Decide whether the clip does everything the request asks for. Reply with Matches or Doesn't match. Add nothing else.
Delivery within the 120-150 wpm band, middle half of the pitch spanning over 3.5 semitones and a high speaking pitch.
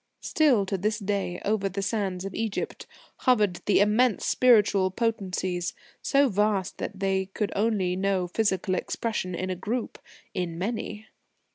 Doesn't match